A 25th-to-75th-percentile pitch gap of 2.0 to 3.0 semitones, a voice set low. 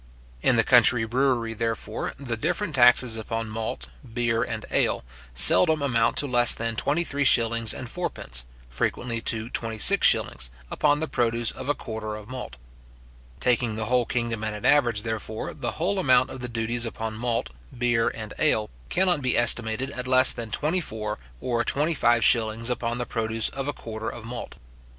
Yes: narrow, 2.5 semitones; low, 120 Hz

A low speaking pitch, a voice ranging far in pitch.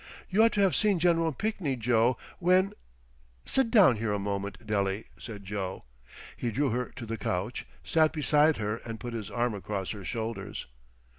Yes: low, 120 Hz; wide, 7.7 semitones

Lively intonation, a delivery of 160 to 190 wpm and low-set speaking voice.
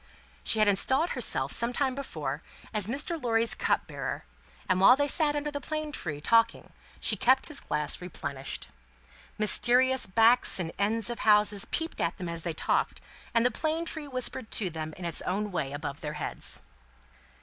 No: wide, 7.2 semitones; average, 180 wpm; high, 225 Hz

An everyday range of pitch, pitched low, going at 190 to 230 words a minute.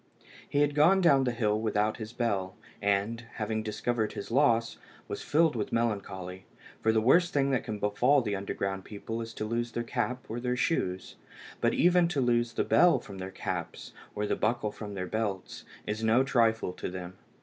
Yes: average, 3.3 semitones; low, 115 Hz; average, 195 wpm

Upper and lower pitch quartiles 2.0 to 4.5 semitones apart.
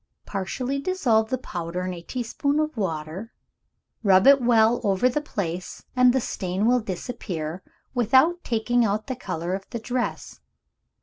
No: average, 5.3 semitones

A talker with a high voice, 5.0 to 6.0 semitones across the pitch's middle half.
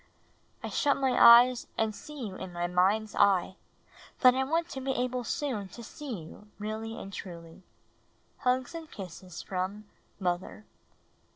Yes: high, 215 Hz; average, 5.3 semitones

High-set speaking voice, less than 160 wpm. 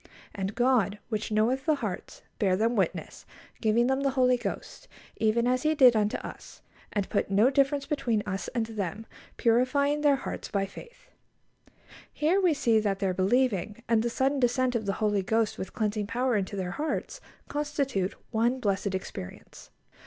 No: high, 230 Hz; average, 170 wpm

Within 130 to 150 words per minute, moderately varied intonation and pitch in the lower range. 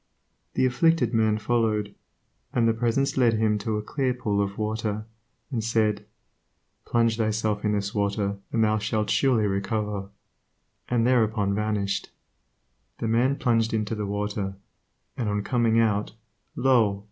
No: average, 145 wpm; narrow, 2.0 semitones; low, 110 Hz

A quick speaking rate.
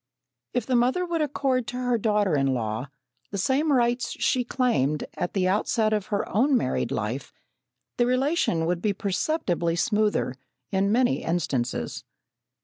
No: average, 150 wpm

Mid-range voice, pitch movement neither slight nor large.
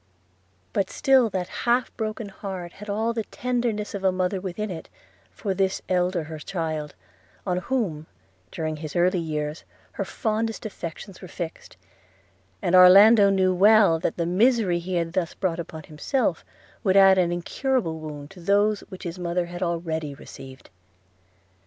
Yes: medium, 180 Hz; average, 3.9 semitones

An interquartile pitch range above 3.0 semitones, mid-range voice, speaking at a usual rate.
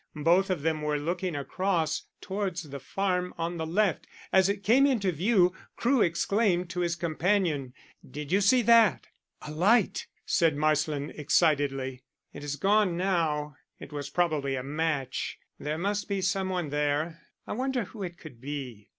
Yes: average, 4.7 semitones; medium, 170 Hz; average, 165 wpm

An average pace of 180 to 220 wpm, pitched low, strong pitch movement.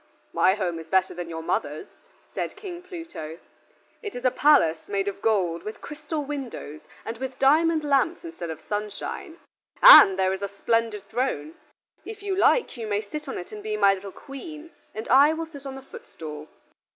No: average, 190 wpm; high, 230 Hz; wide, 8.2 semitones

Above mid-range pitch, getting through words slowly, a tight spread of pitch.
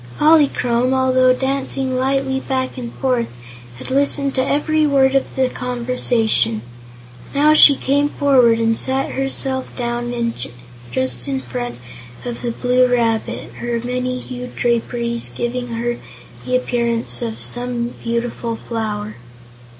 Yes: high, 245 Hz; slow, 125 wpm; narrow, 2.1 semitones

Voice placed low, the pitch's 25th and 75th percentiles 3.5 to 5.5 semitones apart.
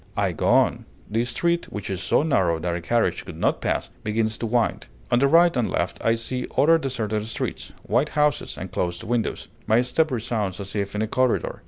Yes: low, 115 Hz; average, 3.8 semitones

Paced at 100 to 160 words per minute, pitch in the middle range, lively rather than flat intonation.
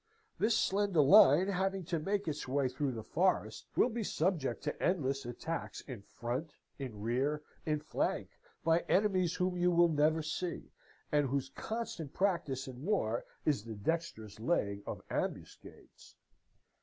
Yes: average, 150 wpm; medium, 150 Hz; wide, 5.7 semitones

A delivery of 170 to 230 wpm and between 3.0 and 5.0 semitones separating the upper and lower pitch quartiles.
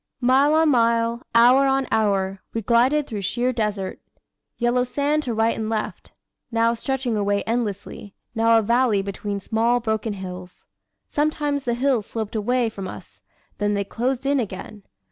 No: average, 160 wpm; average, 3.6 semitones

